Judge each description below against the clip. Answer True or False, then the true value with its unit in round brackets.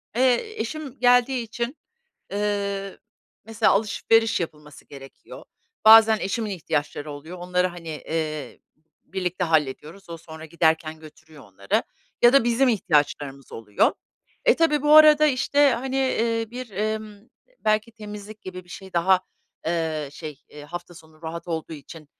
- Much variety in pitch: True (6.4 semitones)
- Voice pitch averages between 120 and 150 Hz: False (190 Hz)